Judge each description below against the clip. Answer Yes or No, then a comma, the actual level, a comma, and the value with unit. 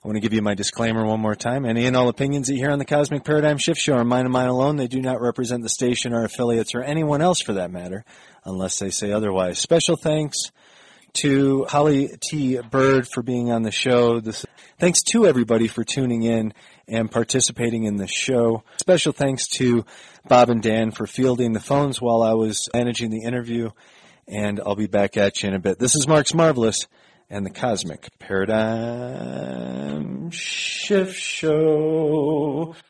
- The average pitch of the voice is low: Yes, low, 120 Hz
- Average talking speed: Yes, average, 190 wpm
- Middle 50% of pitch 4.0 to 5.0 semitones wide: Yes, average, 4.4 semitones